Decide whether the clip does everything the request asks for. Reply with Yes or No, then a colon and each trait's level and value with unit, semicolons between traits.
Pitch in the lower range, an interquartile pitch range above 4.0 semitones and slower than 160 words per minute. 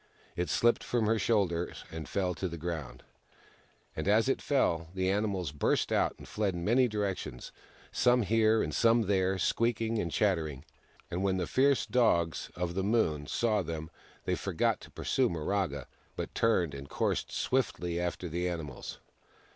No: very low, 95 Hz; average, 4.7 semitones; average, 165 wpm